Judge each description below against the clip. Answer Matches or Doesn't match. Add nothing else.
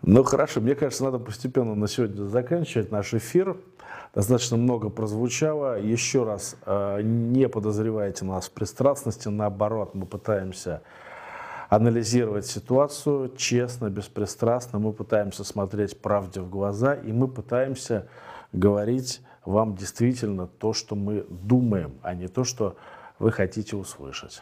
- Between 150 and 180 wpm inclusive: Doesn't match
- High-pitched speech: Doesn't match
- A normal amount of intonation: Matches